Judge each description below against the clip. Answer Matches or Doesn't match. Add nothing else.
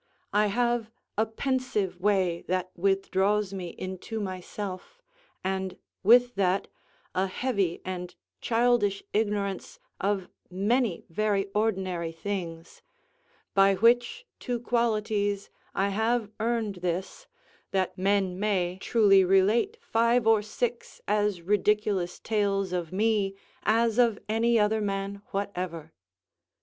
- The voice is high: Matches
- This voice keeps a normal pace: Doesn't match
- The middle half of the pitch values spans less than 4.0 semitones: Matches